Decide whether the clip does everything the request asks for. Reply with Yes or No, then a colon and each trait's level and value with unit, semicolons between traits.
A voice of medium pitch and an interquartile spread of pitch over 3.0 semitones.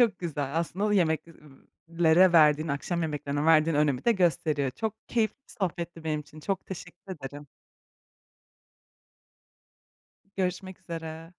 Yes: medium, 165 Hz; average, 3.4 semitones